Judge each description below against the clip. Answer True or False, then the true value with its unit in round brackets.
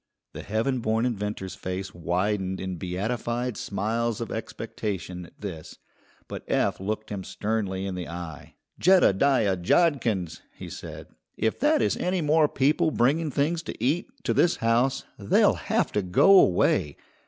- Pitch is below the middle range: True (110 Hz)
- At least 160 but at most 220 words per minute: False (150 wpm)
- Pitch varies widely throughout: True (6.1 semitones)